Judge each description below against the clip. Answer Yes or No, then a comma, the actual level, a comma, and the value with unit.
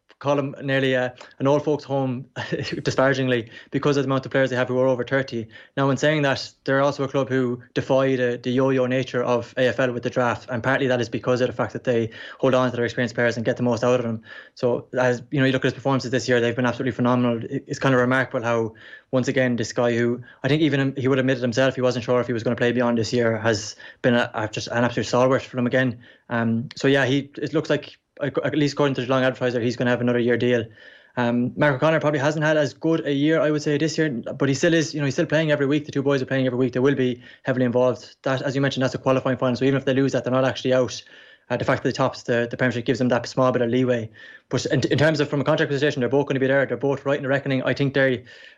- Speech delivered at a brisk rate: Yes, fast, 290 wpm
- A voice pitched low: Yes, low, 130 Hz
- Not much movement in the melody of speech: Yes, narrow, 2.0 semitones